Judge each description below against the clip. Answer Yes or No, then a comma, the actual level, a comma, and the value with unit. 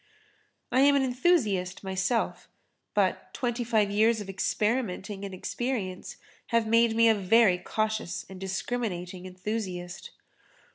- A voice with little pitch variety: No, average, 3.8 semitones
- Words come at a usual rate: No, slow, 115 wpm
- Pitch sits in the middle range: No, high, 215 Hz